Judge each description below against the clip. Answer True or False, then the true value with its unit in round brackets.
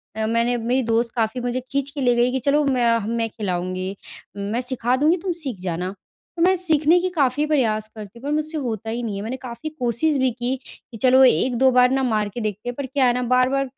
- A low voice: False (250 Hz)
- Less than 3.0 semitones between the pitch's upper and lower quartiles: False (3.3 semitones)